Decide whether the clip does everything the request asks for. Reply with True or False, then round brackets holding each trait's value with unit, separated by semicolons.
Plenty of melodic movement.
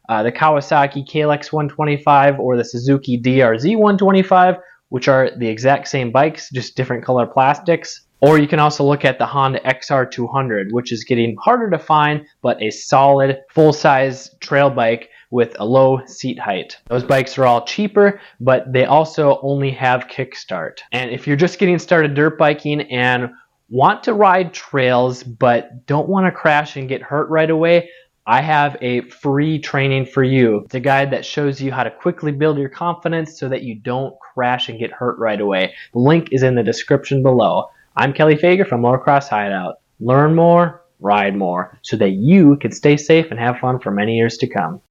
False (3.8 semitones)